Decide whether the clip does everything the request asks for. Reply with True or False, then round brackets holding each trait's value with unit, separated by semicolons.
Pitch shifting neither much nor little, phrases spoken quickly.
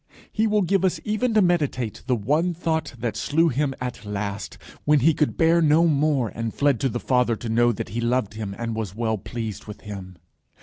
False (6.3 semitones; 215 wpm)